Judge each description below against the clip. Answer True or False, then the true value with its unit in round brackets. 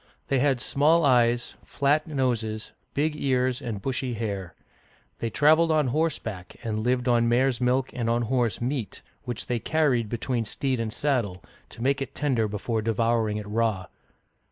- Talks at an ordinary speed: True (160 wpm)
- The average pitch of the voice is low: True (120 Hz)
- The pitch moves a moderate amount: True (3.3 semitones)